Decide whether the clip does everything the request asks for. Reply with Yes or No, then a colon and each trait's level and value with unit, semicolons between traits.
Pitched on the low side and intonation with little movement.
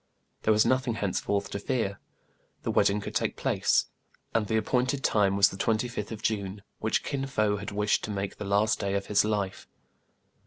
Yes: low, 105 Hz; narrow, 1.9 semitones